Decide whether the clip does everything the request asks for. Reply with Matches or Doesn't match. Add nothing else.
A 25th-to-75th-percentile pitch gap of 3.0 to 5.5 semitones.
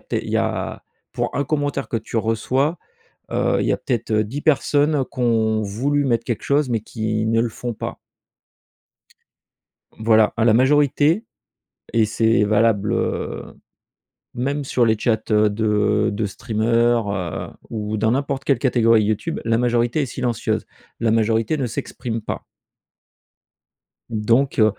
Matches